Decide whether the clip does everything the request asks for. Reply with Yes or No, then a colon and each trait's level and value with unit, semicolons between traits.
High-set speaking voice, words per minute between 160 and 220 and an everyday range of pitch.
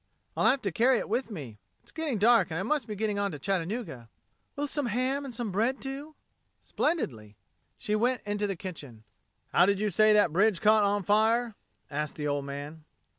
No: high, 210 Hz; average, 200 wpm; wide, 6.4 semitones